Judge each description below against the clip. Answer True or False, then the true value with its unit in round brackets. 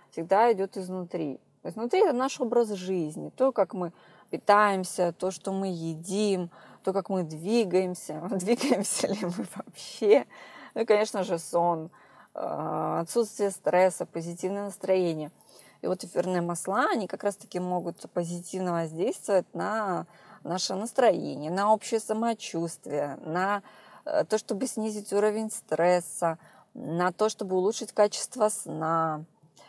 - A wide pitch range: False (3.7 semitones)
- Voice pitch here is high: True (195 Hz)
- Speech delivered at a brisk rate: False (125 wpm)